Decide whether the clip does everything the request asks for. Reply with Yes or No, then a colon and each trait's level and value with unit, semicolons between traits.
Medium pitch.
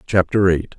No: very low, 90 Hz